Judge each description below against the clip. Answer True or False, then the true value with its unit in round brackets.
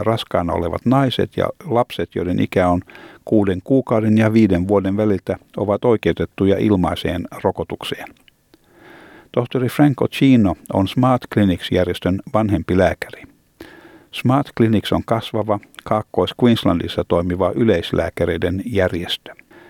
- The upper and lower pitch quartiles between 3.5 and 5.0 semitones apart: True (4.5 semitones)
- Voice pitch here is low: True (105 Hz)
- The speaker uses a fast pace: False (105 wpm)